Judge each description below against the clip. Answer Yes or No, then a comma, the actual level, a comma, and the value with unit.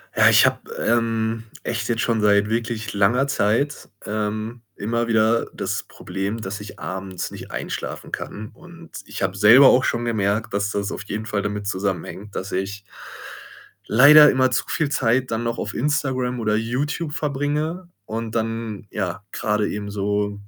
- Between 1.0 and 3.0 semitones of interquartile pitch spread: No, average, 3.4 semitones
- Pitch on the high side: No, low, 110 Hz